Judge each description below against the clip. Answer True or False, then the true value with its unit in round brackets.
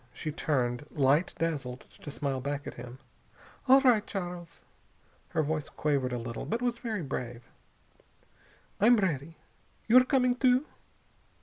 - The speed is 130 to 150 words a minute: True (140 wpm)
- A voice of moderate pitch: True (155 Hz)